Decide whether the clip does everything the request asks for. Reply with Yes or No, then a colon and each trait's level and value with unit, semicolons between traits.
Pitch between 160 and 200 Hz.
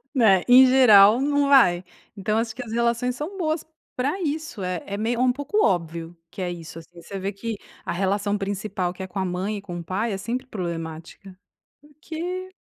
No: high, 210 Hz